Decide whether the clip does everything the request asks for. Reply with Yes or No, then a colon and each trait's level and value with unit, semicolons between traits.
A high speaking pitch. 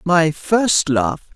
No: medium, 165 Hz